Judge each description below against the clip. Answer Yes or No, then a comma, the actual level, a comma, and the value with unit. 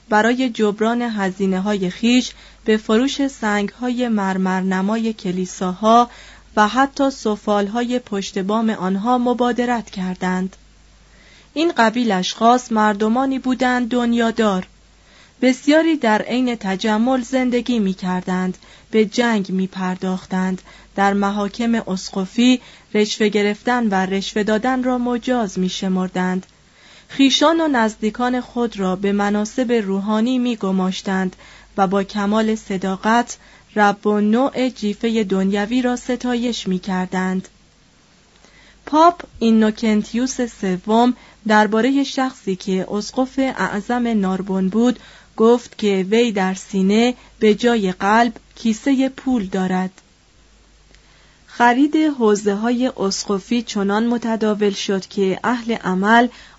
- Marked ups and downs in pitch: No, average, 4.0 semitones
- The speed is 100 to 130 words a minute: Yes, average, 110 wpm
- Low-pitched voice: No, high, 215 Hz